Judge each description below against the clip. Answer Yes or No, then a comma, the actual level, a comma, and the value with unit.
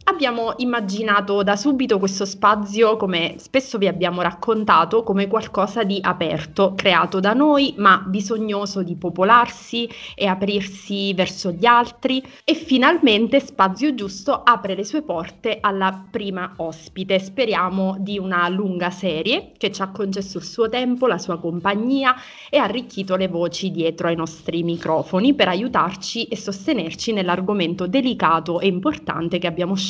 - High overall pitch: Yes, high, 200 Hz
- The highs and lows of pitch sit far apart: No, average, 4.3 semitones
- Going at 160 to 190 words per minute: No, average, 145 wpm